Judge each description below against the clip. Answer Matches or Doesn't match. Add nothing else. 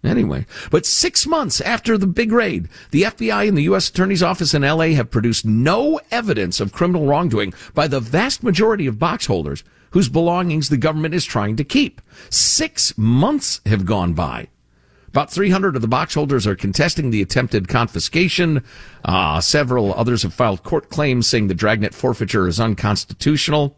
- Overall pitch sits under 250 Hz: Matches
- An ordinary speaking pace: Matches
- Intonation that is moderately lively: Doesn't match